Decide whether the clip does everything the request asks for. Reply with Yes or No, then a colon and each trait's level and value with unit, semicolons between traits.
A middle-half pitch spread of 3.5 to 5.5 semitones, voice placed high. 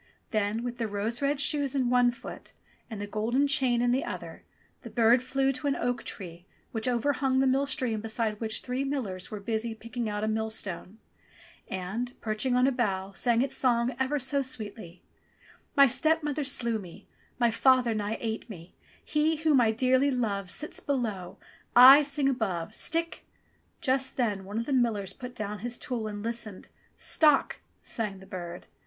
Yes: average, 3.8 semitones; high, 235 Hz